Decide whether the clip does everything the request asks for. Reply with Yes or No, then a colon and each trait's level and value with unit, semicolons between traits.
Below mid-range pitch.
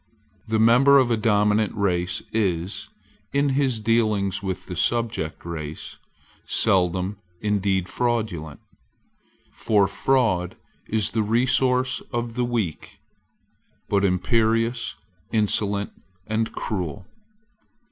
Yes: low, 105 Hz